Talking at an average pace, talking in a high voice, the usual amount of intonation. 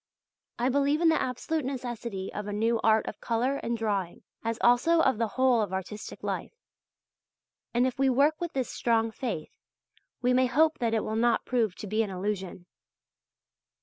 Yes: average, 180 wpm; high, 235 Hz; average, 3.4 semitones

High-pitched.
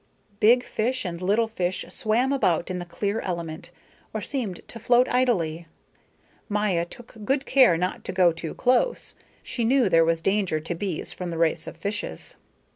Yes: high, 195 Hz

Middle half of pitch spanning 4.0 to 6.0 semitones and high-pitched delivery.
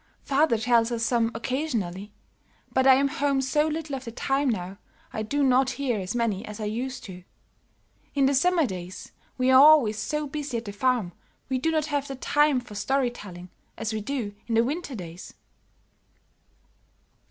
Yes: average, 4.6 semitones; very high, 255 Hz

